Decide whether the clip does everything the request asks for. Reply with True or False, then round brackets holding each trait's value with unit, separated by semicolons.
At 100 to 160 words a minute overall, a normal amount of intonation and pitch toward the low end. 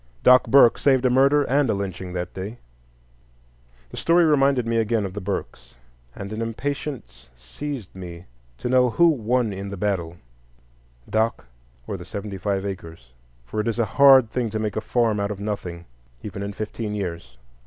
False (180 wpm; 4.7 semitones; 105 Hz)